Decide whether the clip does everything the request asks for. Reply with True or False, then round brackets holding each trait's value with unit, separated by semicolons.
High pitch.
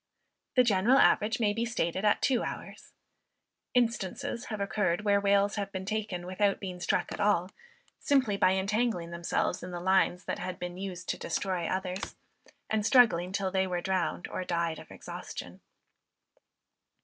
True (195 Hz)